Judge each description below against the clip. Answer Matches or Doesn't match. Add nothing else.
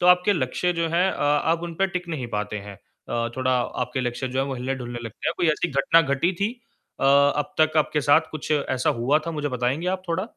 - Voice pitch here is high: Doesn't match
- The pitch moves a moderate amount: Matches